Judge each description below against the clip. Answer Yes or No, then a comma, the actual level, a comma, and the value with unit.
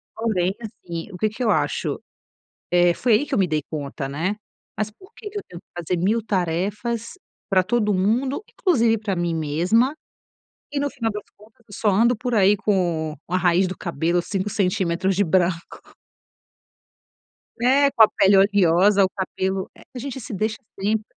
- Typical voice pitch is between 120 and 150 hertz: No, high, 200 Hz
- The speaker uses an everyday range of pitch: Yes, average, 4.1 semitones